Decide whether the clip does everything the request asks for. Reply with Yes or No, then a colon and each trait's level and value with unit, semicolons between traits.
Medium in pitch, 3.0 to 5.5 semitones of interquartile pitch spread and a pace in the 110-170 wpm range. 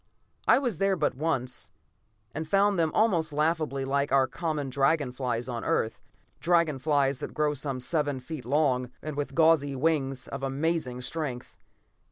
Yes: medium, 145 Hz; average, 3.4 semitones; average, 160 wpm